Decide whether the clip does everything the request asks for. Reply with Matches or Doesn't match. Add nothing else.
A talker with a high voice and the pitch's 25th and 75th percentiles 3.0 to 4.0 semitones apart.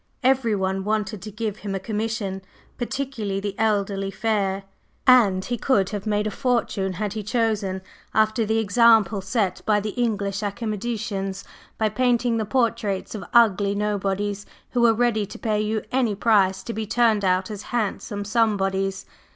Doesn't match